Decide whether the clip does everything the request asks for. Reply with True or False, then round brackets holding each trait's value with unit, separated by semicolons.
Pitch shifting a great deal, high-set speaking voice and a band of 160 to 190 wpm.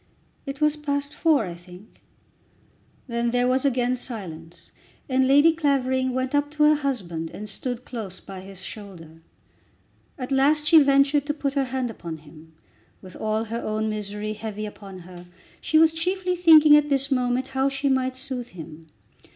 True (5.8 semitones; 255 Hz; 170 wpm)